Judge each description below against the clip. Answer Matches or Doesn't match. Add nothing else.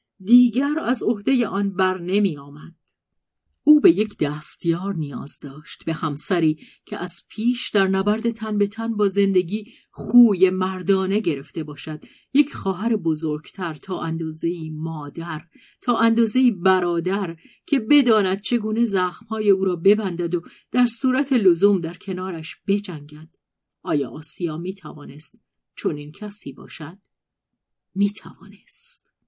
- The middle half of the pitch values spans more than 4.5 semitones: Matches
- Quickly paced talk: Doesn't match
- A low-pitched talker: Doesn't match